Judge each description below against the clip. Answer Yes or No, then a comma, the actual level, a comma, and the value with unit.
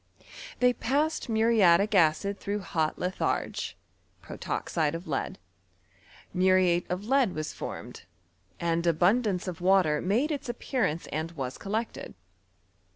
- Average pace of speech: No, slow, 115 wpm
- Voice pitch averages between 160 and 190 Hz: Yes, medium, 185 Hz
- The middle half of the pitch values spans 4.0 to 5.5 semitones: Yes, average, 4.9 semitones